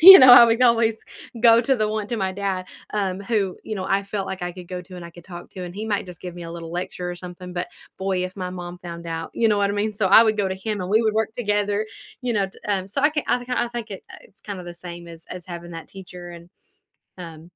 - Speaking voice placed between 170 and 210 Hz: Yes, high, 190 Hz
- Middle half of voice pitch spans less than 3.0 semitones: No, average, 3.4 semitones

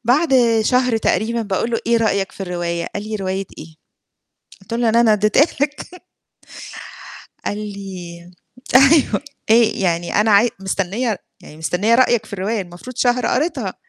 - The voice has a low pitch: No, high, 215 Hz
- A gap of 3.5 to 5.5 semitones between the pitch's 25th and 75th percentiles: Yes, average, 4.1 semitones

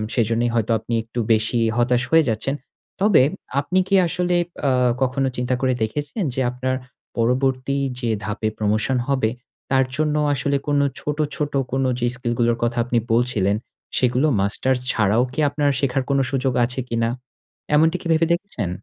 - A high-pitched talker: No, low, 130 Hz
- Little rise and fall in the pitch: No, average, 3.3 semitones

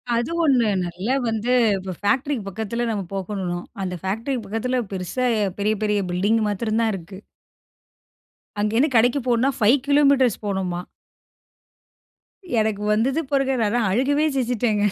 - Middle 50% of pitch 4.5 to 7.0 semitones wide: No, average, 4.0 semitones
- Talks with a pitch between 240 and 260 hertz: No, high, 220 Hz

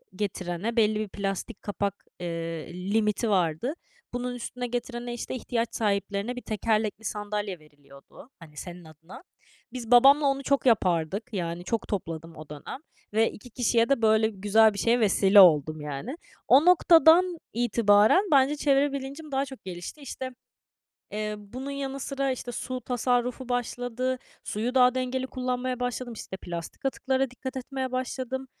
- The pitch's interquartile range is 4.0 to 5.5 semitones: Yes, average, 4.6 semitones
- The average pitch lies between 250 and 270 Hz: No, high, 235 Hz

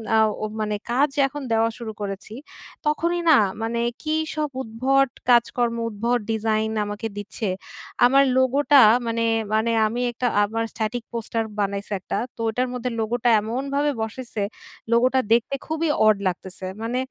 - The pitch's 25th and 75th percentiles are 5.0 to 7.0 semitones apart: No, average, 3.0 semitones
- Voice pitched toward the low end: No, high, 235 Hz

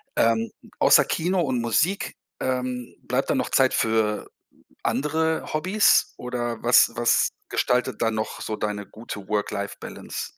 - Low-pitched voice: Yes, low, 120 Hz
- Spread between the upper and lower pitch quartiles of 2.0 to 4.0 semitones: No, average, 4.6 semitones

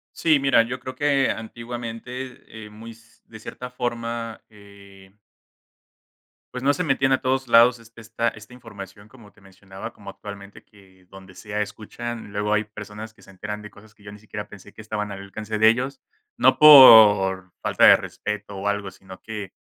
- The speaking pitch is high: No, low, 110 Hz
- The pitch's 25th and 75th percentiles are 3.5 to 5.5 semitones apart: No, average, 2.7 semitones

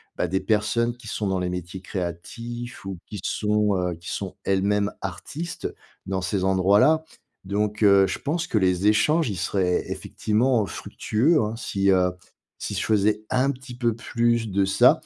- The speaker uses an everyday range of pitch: Yes, average, 3.7 semitones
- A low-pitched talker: Yes, low, 105 Hz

